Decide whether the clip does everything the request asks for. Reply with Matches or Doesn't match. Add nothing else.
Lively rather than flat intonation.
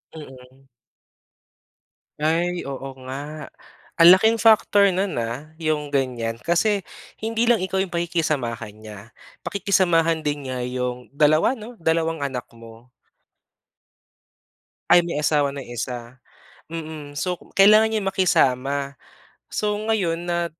Matches